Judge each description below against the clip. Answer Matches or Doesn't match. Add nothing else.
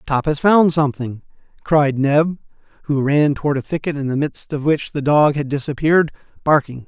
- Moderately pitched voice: Matches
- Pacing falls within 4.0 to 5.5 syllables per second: Matches